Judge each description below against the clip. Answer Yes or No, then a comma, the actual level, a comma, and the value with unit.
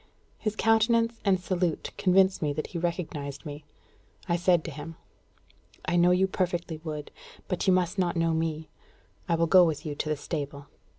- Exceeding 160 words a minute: Yes, average, 180 wpm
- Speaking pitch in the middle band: Yes, medium, 170 Hz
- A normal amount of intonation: Yes, average, 3.1 semitones